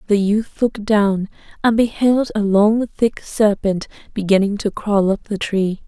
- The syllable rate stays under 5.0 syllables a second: Yes, 4.2 syllables/s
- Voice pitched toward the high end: Yes, high, 210 Hz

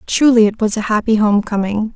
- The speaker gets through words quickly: Yes, fast, 215 wpm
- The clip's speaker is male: No, female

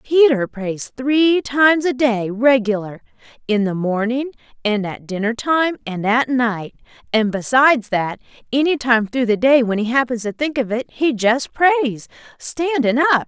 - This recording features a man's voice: No, female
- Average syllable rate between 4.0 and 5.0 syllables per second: Yes, 4.3 syllables/s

